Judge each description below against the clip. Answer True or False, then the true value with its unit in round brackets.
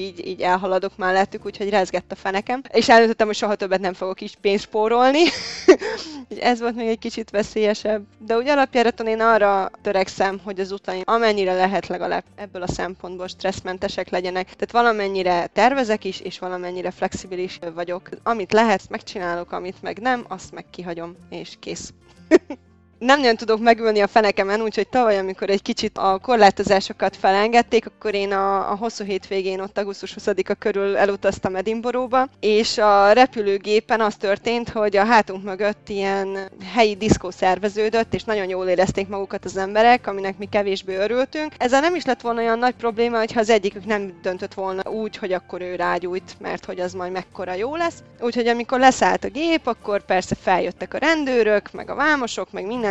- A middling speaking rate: False (170 wpm)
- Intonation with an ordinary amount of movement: True (3.2 semitones)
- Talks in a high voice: True (205 Hz)